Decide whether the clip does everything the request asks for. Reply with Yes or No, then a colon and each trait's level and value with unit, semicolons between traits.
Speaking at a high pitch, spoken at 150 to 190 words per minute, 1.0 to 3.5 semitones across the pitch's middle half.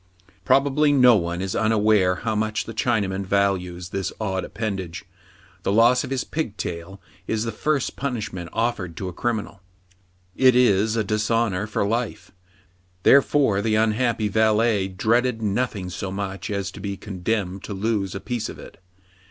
No: low, 105 Hz; average, 155 wpm; average, 3.2 semitones